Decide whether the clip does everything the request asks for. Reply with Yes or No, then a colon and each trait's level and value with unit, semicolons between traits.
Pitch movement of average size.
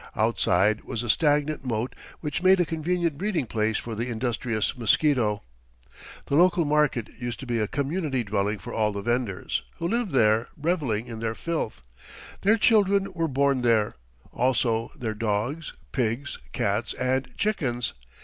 No: wide, 5.8 semitones